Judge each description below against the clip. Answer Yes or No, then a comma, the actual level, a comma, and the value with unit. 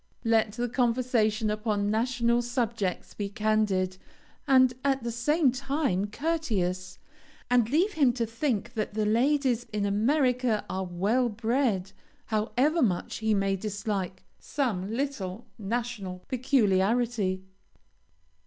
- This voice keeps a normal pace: No, slow, 115 wpm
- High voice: Yes, high, 225 Hz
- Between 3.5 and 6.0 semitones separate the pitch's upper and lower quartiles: Yes, average, 3.8 semitones